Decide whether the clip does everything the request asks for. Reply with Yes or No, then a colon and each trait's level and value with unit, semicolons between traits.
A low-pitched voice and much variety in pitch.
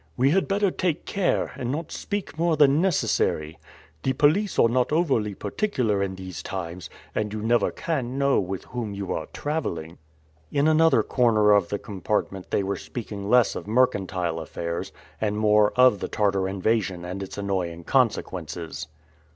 Yes: low, 105 Hz; wide, 6.5 semitones